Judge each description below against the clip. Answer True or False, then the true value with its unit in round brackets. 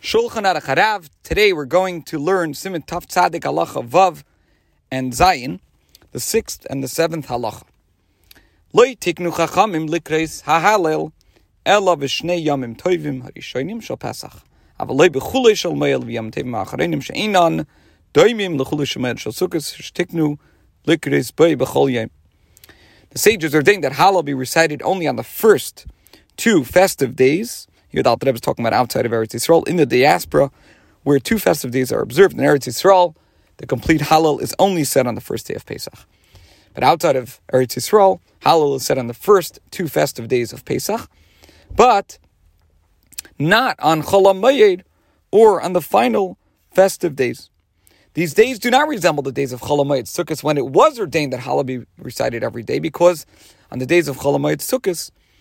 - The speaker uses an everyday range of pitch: False (7.4 semitones)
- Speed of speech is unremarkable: True (170 wpm)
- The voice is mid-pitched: True (145 Hz)